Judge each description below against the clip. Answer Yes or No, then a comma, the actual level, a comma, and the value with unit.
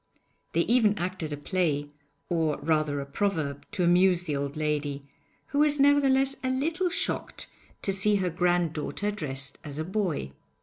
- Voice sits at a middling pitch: Yes, medium, 175 Hz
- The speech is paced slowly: No, average, 160 wpm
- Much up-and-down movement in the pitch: Yes, wide, 5.9 semitones